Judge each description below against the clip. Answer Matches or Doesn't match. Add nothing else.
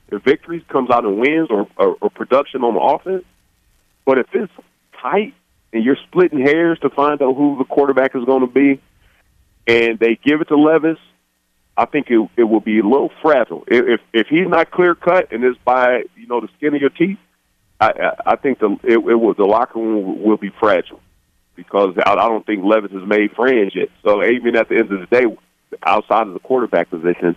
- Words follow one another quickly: Matches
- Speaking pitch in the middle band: Doesn't match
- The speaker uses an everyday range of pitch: Doesn't match